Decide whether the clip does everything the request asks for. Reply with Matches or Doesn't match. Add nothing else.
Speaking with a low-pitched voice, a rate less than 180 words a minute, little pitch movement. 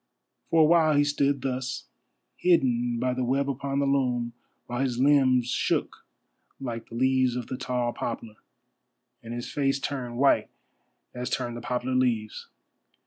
Matches